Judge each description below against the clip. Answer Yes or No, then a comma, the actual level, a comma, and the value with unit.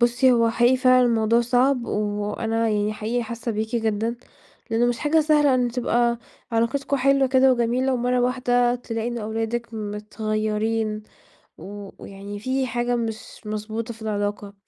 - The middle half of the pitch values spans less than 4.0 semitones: Yes, narrow, 2.4 semitones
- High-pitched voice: Yes, high, 235 Hz